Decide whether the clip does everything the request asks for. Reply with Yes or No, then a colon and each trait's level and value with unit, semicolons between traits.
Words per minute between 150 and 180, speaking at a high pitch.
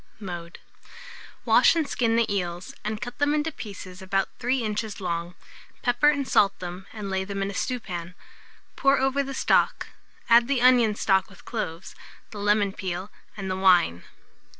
Yes: average, 170 wpm; high, 205 Hz